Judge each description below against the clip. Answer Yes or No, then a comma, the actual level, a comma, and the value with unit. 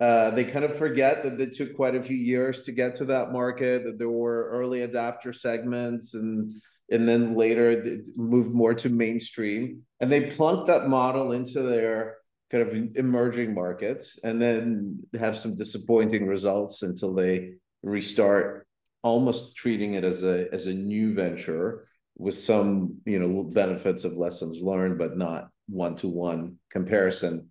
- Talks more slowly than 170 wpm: Yes, average, 160 wpm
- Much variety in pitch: No, average, 3.8 semitones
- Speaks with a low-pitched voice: Yes, low, 115 Hz